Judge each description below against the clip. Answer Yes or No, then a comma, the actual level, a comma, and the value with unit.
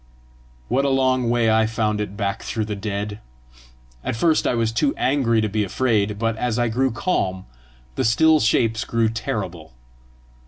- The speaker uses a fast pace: No, average, 170 wpm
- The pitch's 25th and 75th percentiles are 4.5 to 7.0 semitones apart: No, average, 2.8 semitones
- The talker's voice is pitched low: Yes, low, 115 Hz